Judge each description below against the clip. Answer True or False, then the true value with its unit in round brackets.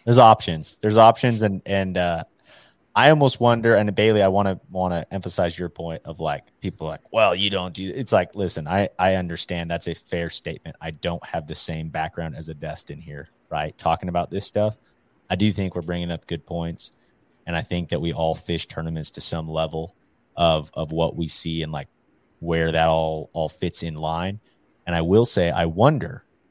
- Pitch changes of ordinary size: True (3.2 semitones)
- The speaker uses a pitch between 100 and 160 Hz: False (85 Hz)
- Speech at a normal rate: False (215 wpm)